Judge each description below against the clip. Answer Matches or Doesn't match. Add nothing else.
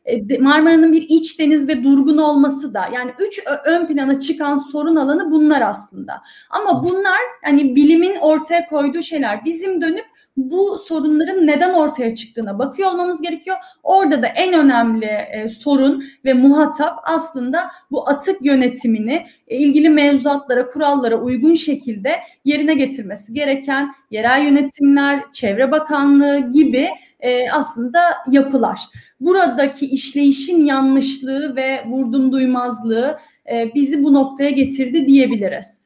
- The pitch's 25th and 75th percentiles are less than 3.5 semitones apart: Matches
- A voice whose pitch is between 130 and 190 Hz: Doesn't match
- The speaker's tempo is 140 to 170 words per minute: Doesn't match